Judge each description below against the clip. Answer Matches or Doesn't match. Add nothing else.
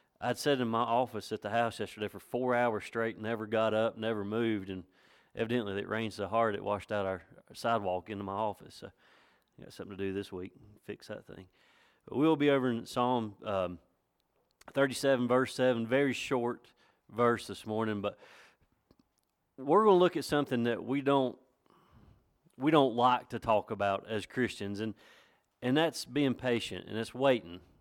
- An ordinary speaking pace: Matches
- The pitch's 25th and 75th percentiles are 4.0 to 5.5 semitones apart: Doesn't match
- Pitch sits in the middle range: Doesn't match